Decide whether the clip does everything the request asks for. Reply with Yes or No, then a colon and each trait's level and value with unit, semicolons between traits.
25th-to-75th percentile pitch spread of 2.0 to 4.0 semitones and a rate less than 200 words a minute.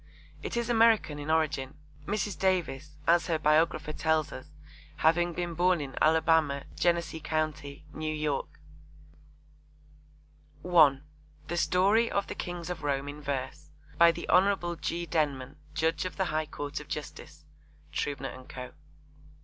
Yes: average, 3.0 semitones; average, 140 wpm